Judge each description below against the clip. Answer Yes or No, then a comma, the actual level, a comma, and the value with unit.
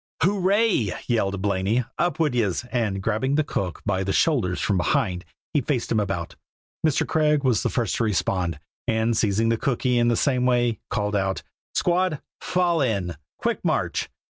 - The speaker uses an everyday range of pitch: No, wide, 6.5 semitones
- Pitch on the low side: Yes, low, 115 Hz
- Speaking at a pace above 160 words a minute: Yes, average, 170 wpm